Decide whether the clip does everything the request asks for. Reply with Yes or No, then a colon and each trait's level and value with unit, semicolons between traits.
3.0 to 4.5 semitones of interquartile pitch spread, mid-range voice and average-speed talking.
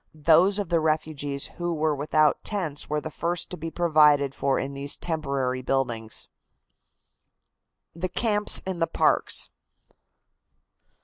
No: average, 3.4 semitones; medium, 155 Hz; slow, 130 wpm